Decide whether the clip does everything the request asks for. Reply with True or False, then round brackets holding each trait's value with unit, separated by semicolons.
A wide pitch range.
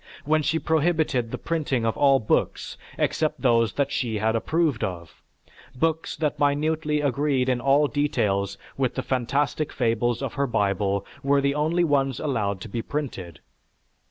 False (4.7 semitones)